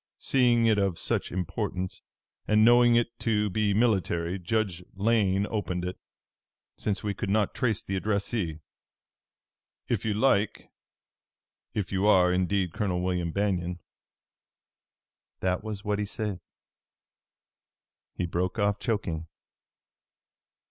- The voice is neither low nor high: No, low, 100 Hz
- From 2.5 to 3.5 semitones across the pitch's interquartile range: Yes, average, 3.0 semitones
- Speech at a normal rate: No, slow, 120 wpm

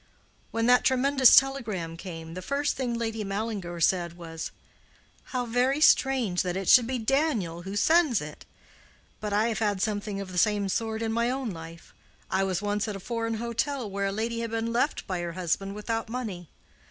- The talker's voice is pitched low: No, high, 215 Hz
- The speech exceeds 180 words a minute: Yes, average, 190 wpm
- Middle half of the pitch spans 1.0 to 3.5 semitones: No, average, 4.2 semitones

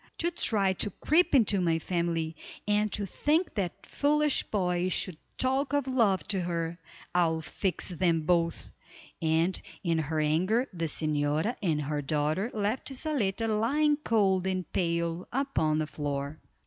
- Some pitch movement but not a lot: No, wide, 5.7 semitones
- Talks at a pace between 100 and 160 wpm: Yes, average, 150 wpm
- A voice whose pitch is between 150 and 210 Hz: Yes, medium, 185 Hz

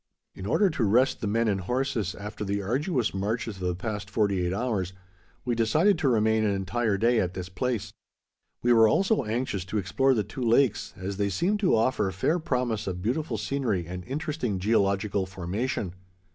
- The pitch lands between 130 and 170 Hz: No, low, 110 Hz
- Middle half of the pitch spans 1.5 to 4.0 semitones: No, average, 4.5 semitones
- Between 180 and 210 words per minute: Yes, average, 185 wpm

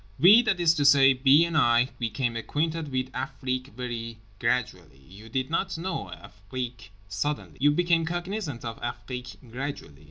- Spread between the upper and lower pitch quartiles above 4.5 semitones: Yes, average, 5.3 semitones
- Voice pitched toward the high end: No, low, 130 Hz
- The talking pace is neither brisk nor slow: Yes, average, 155 wpm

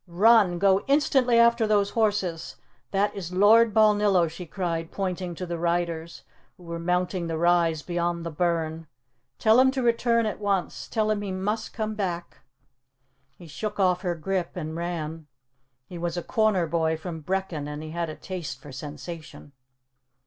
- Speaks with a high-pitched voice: No, medium, 180 Hz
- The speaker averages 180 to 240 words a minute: No, average, 170 wpm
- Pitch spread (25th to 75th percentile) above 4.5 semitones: No, average, 3.8 semitones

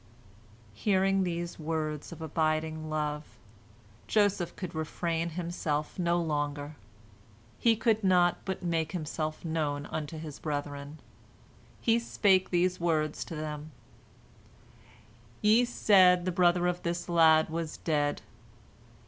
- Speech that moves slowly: Yes, slow, 115 wpm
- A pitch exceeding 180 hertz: No, medium, 165 Hz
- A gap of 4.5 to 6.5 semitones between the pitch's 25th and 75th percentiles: No, average, 2.8 semitones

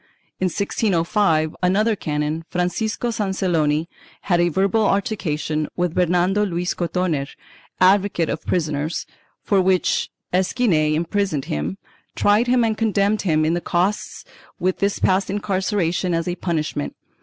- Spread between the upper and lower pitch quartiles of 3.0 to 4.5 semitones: Yes, average, 3.8 semitones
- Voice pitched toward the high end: No, medium, 180 Hz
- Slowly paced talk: Yes, slow, 130 wpm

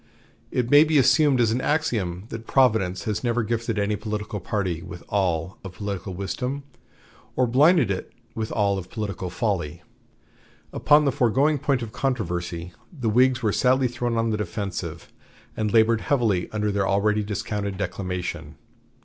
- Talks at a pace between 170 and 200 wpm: No, average, 160 wpm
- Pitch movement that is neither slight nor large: Yes, average, 4.5 semitones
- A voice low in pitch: Yes, low, 105 Hz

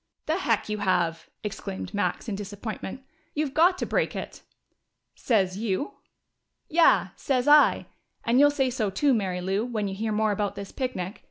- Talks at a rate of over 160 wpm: Yes, average, 170 wpm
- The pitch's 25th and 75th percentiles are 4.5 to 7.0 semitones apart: Yes, average, 5.2 semitones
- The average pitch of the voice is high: Yes, high, 215 Hz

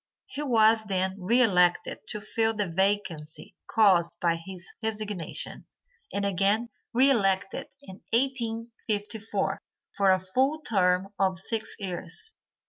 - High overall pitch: Yes, high, 205 Hz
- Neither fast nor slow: No, slow, 125 wpm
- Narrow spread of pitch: No, average, 3.3 semitones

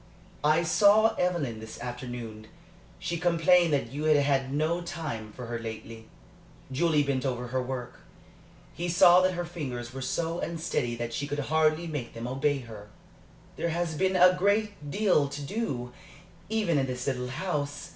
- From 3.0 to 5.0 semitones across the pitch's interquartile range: No, wide, 5.6 semitones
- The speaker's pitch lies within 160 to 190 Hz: No, medium, 145 Hz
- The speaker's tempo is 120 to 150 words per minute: No, average, 165 wpm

